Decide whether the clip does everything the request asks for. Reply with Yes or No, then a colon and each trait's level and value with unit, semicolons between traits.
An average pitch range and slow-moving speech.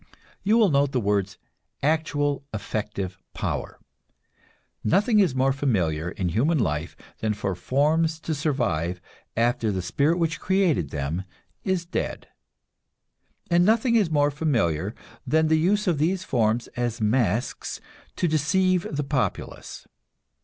No: wide, 7.8 semitones; slow, 130 wpm